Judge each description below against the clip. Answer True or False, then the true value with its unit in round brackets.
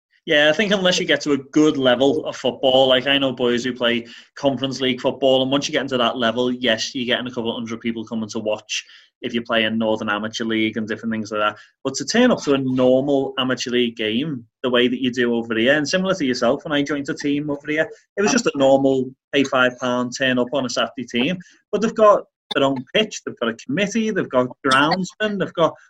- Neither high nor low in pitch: False (130 Hz)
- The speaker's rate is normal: False (250 wpm)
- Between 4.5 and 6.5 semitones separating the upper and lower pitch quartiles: False (3.4 semitones)